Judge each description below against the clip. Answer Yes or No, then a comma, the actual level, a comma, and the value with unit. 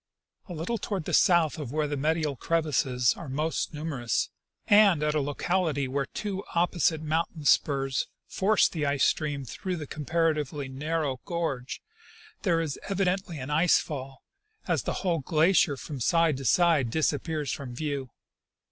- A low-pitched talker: No, medium, 155 Hz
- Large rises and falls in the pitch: No, average, 3.4 semitones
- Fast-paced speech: No, average, 155 wpm